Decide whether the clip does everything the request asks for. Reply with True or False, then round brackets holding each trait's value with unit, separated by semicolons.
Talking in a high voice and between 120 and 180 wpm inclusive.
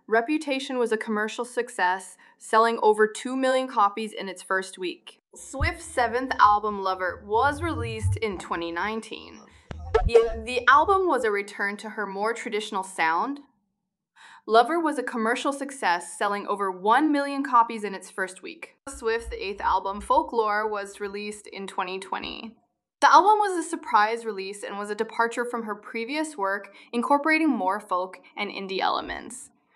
True (220 Hz; 150 wpm)